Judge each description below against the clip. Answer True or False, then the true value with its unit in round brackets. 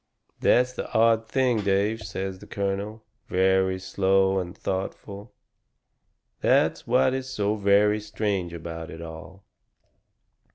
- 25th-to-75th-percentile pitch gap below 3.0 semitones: True (2.4 semitones)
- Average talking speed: False (120 wpm)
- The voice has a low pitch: True (100 Hz)